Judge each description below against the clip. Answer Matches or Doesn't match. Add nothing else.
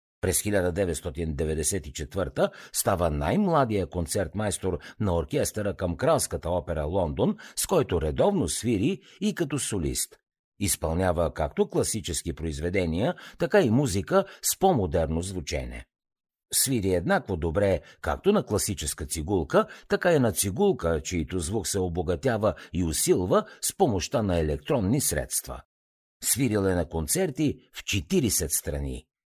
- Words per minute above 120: Doesn't match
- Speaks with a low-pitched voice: Matches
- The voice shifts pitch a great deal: Doesn't match